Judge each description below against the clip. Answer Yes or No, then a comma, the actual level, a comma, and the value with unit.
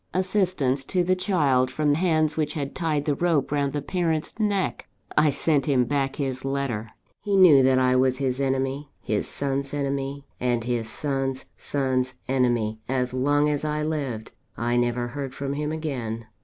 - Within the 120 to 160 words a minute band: No, average, 170 wpm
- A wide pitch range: No, average, 2.8 semitones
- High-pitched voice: No, medium, 140 Hz